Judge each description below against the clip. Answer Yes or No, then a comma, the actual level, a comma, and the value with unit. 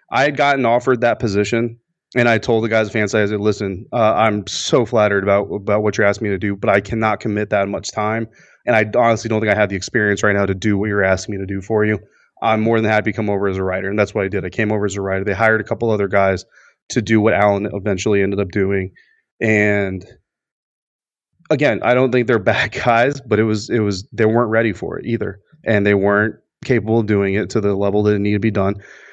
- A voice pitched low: Yes, low, 105 Hz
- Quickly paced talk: Yes, fast, 260 wpm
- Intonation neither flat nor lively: No, narrow, 2.0 semitones